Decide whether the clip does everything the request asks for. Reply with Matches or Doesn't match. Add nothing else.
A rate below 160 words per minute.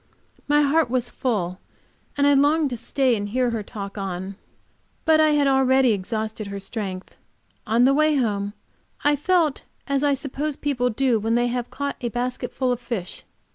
Doesn't match